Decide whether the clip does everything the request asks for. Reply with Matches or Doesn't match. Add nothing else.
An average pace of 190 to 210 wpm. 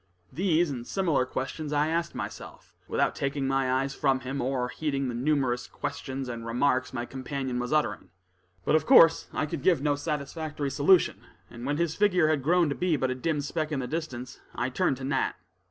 Matches